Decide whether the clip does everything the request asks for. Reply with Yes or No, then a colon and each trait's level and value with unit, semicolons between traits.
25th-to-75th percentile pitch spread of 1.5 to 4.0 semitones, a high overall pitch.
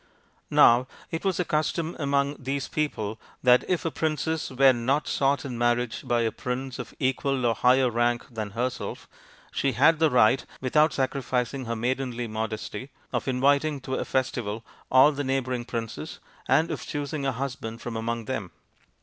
No: average, 2.9 semitones; low, 130 Hz